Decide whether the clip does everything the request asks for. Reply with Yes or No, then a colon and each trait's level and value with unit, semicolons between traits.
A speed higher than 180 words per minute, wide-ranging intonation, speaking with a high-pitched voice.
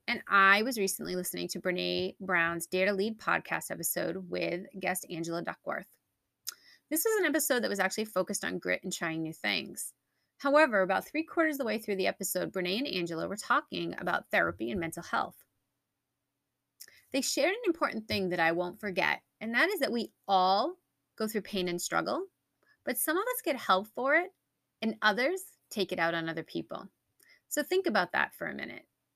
Yes: average, 195 wpm; wide, 8.0 semitones; high, 200 Hz